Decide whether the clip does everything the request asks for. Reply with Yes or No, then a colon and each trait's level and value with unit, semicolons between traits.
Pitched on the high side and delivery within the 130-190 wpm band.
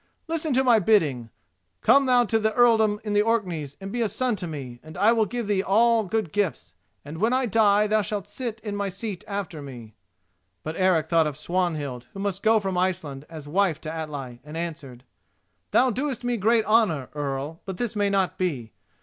No: high, 195 Hz; average, 200 wpm